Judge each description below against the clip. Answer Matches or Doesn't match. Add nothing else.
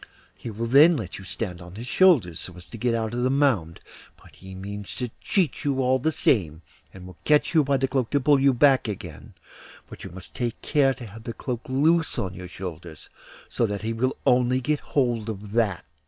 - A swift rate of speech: Matches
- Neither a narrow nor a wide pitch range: Doesn't match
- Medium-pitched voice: Doesn't match